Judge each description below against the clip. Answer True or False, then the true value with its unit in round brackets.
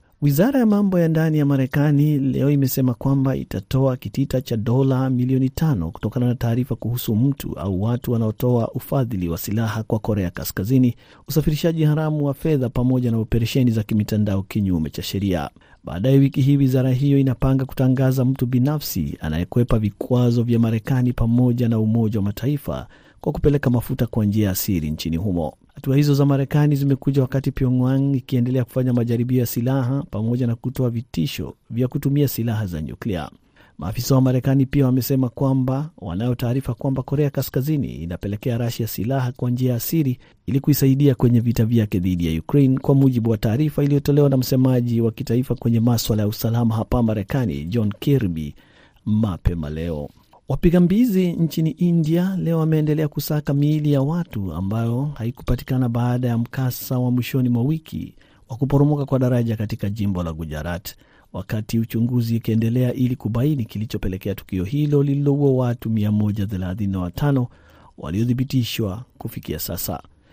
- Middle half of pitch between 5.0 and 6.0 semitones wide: False (3.9 semitones)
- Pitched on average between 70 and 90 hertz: False (125 Hz)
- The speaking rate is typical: False (150 wpm)